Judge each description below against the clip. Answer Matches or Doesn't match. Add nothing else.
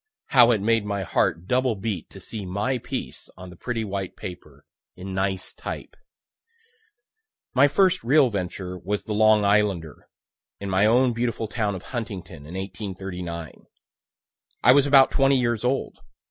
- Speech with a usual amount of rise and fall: Matches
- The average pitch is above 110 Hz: Doesn't match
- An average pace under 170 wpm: Matches